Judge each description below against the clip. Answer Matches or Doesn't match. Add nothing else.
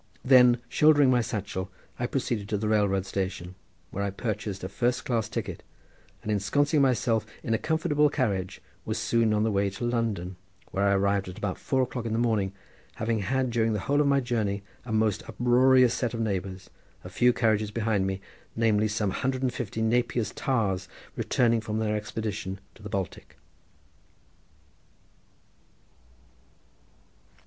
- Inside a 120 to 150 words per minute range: Doesn't match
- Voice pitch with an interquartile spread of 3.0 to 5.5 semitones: Matches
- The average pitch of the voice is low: Matches